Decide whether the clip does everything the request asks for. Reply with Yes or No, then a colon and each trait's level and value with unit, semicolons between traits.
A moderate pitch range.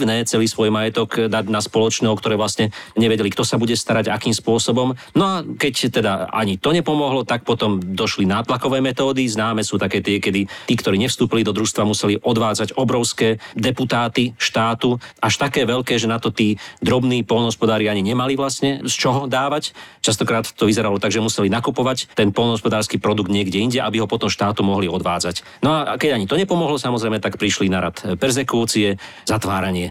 Yes: average, 3.1 semitones